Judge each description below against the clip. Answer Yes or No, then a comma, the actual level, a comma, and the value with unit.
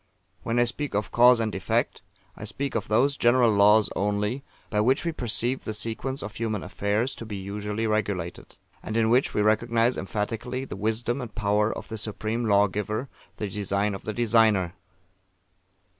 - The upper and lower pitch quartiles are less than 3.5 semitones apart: Yes, narrow, 2.5 semitones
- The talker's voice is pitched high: No, low, 110 Hz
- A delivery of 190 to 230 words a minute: No, average, 175 wpm